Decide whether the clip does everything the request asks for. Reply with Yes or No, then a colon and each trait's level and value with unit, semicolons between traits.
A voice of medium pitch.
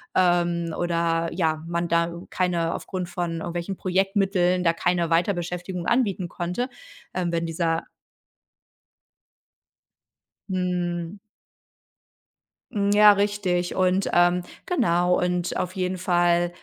Yes: medium, 175 Hz